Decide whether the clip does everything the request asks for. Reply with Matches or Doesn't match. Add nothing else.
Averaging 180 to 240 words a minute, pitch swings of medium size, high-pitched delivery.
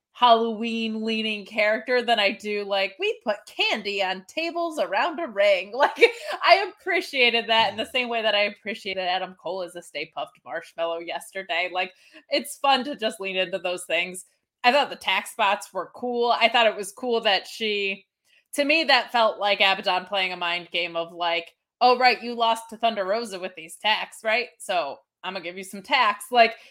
Matches